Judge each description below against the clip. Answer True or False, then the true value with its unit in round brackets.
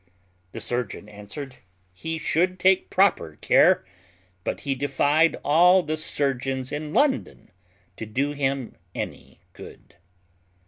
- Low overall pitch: False (145 Hz)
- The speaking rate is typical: False (120 wpm)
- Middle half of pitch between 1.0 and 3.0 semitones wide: False (4.1 semitones)